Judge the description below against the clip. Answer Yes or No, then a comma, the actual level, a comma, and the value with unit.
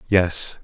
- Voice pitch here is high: No, very low, 95 Hz